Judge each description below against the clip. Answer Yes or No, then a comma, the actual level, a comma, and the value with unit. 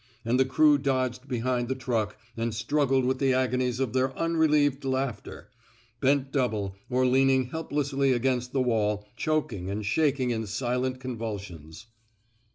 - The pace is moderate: Yes, average, 150 wpm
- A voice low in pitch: Yes, low, 130 Hz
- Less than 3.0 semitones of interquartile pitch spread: Yes, narrow, 2.6 semitones